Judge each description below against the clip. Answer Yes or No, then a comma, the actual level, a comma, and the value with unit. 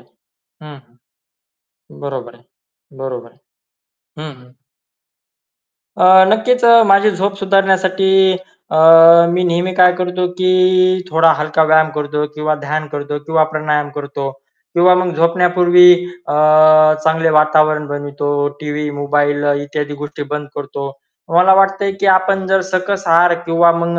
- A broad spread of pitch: No, average, 3.9 semitones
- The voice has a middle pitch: Yes, medium, 160 Hz